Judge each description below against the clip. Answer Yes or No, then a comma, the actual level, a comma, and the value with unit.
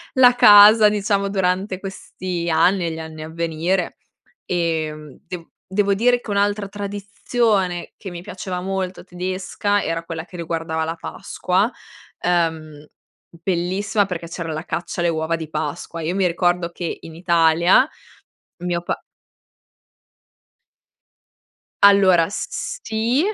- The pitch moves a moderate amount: Yes, average, 3.1 semitones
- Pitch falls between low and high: Yes, medium, 180 Hz